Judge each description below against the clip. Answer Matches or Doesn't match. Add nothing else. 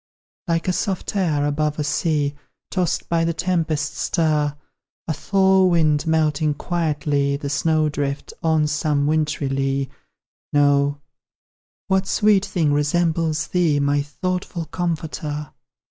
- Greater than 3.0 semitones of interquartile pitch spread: Doesn't match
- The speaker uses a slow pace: Matches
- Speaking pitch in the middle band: Matches